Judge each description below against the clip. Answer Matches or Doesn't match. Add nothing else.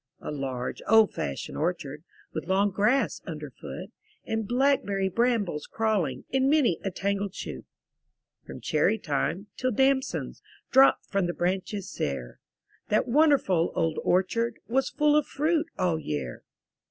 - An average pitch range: Doesn't match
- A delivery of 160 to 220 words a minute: Doesn't match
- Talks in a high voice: Matches